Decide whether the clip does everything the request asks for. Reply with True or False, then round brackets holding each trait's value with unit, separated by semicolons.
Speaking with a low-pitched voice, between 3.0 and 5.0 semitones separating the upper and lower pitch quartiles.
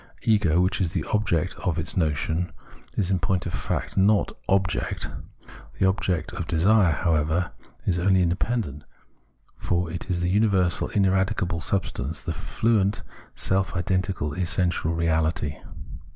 False (90 Hz; 2.5 semitones)